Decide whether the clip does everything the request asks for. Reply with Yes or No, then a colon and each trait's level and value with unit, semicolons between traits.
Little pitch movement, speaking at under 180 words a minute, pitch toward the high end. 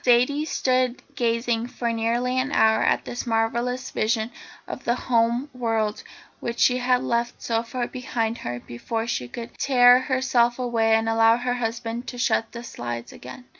Yes: narrow, 1.8 semitones; average, 170 wpm; high, 235 Hz